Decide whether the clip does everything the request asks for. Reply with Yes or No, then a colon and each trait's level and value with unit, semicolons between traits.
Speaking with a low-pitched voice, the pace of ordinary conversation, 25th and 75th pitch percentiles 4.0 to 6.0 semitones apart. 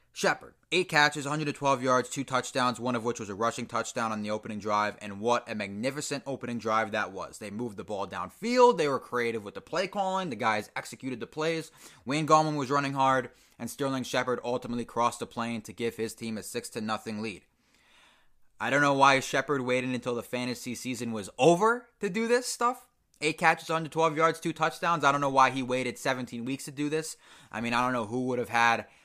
No: low, 125 Hz; fast, 220 wpm; average, 4.3 semitones